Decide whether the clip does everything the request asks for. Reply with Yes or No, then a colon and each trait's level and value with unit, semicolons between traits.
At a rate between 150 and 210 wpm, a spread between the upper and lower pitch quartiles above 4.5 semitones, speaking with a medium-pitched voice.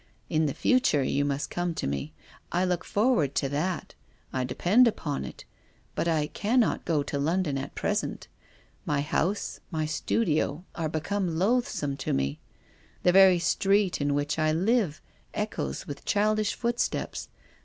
Yes: average, 155 wpm; wide, 5.5 semitones; medium, 160 Hz